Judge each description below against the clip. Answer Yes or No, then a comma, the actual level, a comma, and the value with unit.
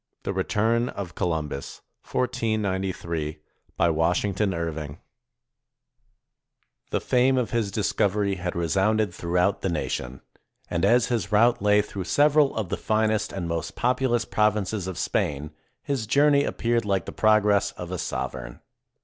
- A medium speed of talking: No, slow, 130 wpm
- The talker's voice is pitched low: Yes, low, 100 Hz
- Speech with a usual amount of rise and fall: Yes, average, 4.7 semitones